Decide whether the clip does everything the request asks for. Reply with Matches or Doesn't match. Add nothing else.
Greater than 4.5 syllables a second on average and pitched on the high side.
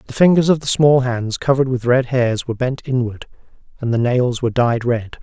Doesn't match